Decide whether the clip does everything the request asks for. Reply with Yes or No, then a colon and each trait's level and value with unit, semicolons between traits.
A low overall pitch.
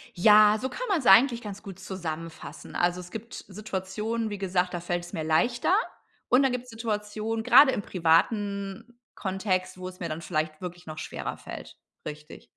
No: high, 195 Hz